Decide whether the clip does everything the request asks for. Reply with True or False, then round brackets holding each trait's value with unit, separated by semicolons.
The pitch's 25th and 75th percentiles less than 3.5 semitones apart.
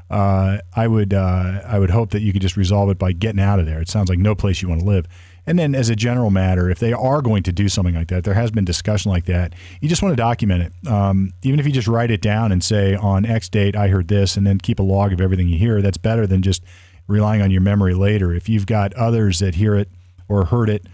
True (2.5 semitones)